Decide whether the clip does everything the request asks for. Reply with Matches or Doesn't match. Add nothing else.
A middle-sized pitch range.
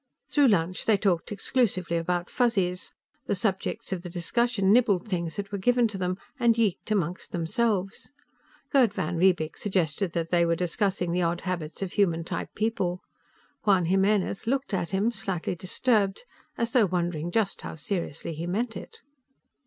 Matches